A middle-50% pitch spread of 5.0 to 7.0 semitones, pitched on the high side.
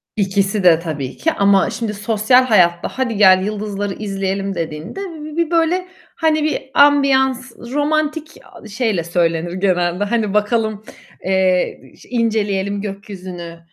Yes: wide, 5.6 semitones; high, 205 Hz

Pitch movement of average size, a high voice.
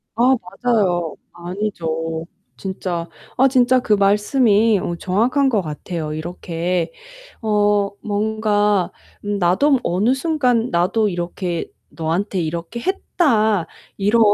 Yes: average, 4.7 semitones; high, 205 Hz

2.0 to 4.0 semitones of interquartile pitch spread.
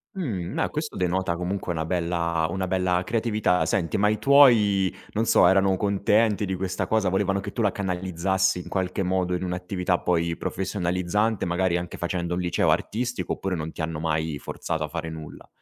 Yes: narrow, 2.4 semitones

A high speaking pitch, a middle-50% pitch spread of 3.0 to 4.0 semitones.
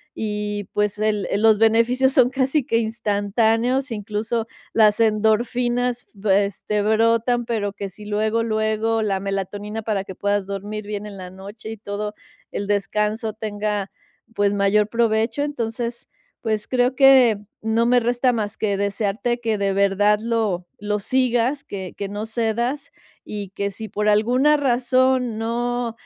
No: high, 220 Hz; narrow, 2.5 semitones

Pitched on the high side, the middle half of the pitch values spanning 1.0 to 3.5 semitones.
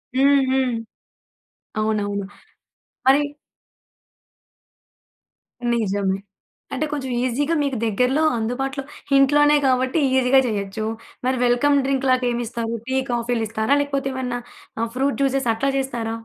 Yes: very high, 255 Hz; average, 3.1 semitones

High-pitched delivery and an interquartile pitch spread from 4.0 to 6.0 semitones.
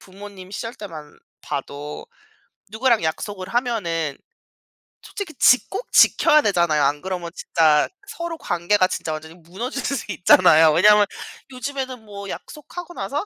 No: high, 200 Hz; wide, 7.3 semitones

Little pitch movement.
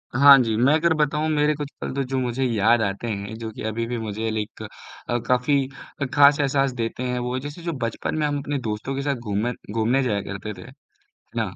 No: average, 4.2 semitones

